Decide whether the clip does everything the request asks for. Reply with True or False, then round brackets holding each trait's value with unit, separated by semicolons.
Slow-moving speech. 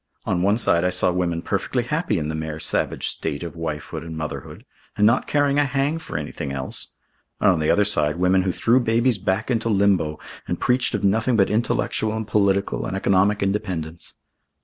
False (195 wpm)